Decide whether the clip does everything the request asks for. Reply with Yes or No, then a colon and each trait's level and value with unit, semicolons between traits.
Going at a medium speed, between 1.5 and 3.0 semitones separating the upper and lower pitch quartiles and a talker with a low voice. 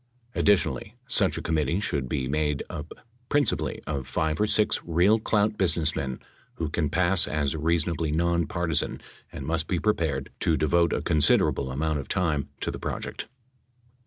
Yes: average, 170 wpm; average, 2.7 semitones; very low, 80 Hz